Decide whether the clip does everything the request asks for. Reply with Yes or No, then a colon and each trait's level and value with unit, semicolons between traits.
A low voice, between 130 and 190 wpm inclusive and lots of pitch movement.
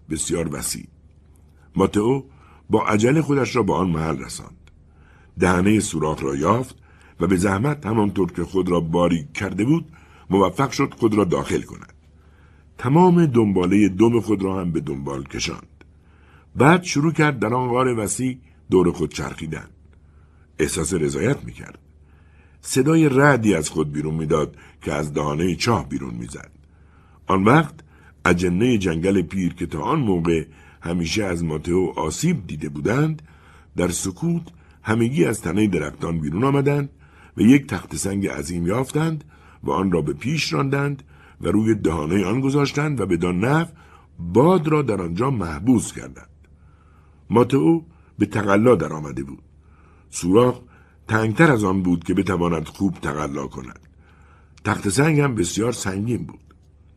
Yes: very low, 90 Hz; average, 145 wpm; wide, 7.3 semitones